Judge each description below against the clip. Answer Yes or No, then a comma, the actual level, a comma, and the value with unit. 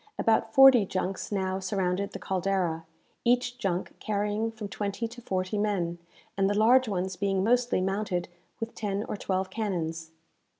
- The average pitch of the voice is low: No, high, 200 Hz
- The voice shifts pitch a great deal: No, average, 2.9 semitones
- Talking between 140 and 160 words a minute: Yes, average, 155 wpm